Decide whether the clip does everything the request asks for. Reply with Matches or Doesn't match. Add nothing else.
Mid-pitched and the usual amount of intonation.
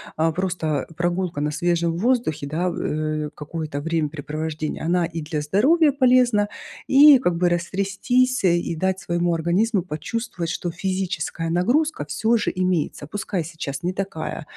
Matches